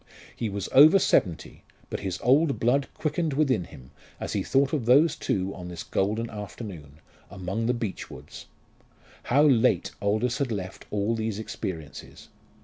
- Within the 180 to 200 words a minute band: No, average, 155 wpm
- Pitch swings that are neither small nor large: No, wide, 5.8 semitones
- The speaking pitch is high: No, low, 110 Hz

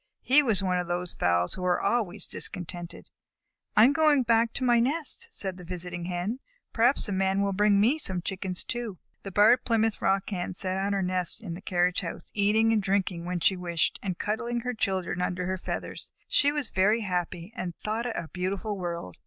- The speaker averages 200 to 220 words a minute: Yes, fast, 205 wpm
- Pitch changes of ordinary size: Yes, average, 3.9 semitones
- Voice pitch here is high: Yes, high, 195 Hz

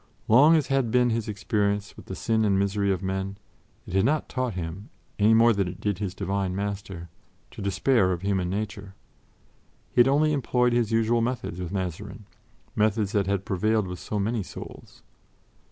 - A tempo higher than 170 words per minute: Yes, average, 185 wpm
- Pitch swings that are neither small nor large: Yes, average, 3.1 semitones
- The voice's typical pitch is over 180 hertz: No, low, 100 Hz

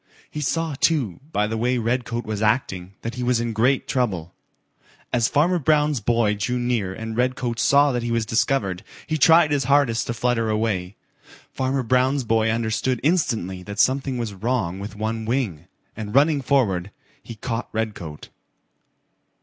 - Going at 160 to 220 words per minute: Yes, average, 165 wpm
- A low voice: Yes, low, 115 Hz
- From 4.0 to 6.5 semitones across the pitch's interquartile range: No, average, 3.6 semitones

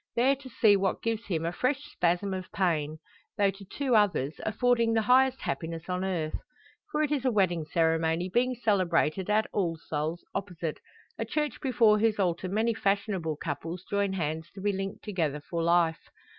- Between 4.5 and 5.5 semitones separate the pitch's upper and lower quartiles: Yes, average, 5.0 semitones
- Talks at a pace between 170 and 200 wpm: Yes, average, 180 wpm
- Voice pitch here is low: No, high, 190 Hz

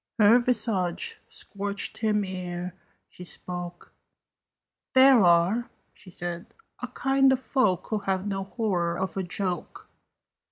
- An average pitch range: Yes, average, 4.1 semitones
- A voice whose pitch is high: Yes, high, 195 Hz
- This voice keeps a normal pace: No, slow, 125 wpm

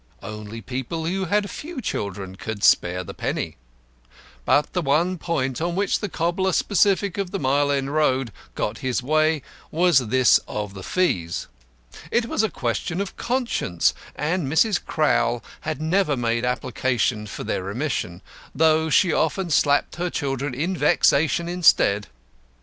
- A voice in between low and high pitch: Yes, medium, 150 Hz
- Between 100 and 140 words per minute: No, average, 150 wpm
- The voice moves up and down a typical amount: No, wide, 6.7 semitones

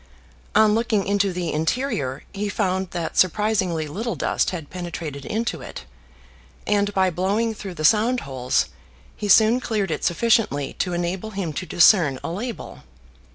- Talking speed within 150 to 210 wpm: Yes, average, 155 wpm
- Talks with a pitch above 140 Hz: Yes, high, 190 Hz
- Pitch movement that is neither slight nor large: Yes, average, 4.3 semitones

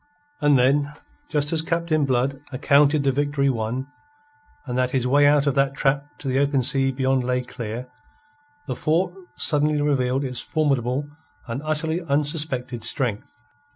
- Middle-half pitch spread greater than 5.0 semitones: No, narrow, 2.5 semitones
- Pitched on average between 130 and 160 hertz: Yes, medium, 140 Hz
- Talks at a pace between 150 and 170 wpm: Yes, average, 155 wpm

